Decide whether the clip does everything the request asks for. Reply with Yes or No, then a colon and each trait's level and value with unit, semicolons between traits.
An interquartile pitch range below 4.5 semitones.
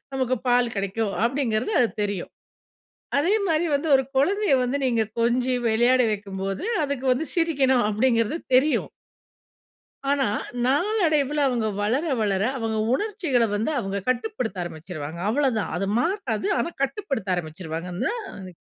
No: wide, 5.6 semitones